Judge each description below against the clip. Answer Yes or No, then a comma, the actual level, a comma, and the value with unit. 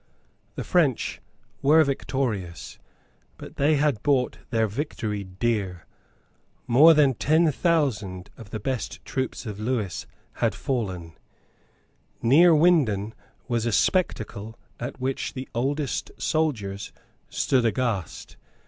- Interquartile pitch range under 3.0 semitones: No, wide, 5.6 semitones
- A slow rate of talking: Yes, slow, 110 wpm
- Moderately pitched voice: No, low, 125 Hz